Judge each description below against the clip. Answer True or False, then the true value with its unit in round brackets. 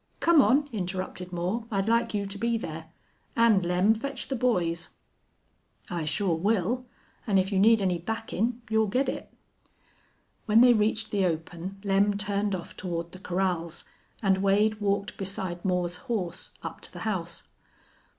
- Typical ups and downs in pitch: True (3.7 semitones)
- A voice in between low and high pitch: False (200 Hz)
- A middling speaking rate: True (160 wpm)